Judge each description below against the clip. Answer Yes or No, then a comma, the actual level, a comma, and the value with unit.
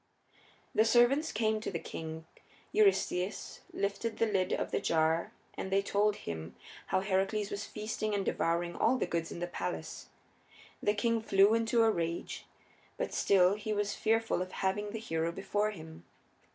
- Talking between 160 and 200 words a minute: Yes, average, 165 wpm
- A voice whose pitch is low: No, high, 200 Hz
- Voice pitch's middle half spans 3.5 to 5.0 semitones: Yes, average, 4.0 semitones